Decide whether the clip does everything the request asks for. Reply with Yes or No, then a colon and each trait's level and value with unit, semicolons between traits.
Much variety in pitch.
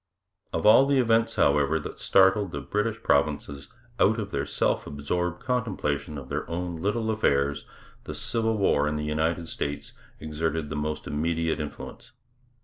Yes: wide, 6.1 semitones